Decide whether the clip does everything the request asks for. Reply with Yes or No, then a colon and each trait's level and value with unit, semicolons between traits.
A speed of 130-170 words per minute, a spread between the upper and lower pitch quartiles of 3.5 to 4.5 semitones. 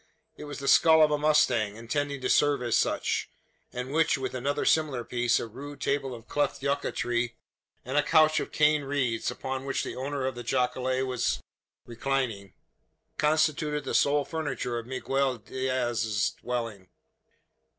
No: average, 160 wpm; average, 3.1 semitones